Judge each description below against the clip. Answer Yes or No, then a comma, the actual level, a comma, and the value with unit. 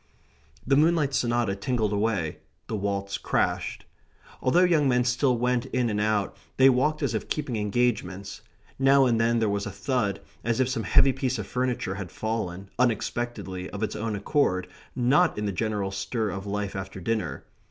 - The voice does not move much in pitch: No, average, 4.1 semitones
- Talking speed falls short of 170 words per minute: No, average, 175 wpm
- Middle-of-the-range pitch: No, low, 115 Hz